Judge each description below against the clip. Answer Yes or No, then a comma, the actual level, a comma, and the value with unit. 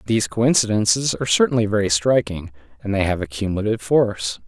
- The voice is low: Yes, low, 105 Hz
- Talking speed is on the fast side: No, average, 160 wpm